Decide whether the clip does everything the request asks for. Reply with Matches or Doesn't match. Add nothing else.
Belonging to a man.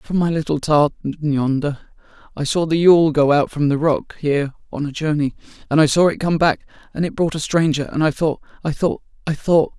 Matches